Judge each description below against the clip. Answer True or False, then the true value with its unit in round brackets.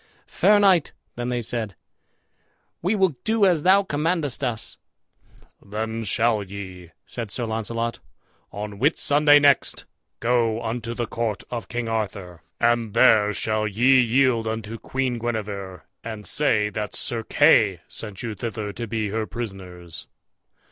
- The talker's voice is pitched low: True (115 Hz)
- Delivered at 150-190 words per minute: False (140 wpm)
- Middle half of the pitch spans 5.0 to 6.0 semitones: False (3.2 semitones)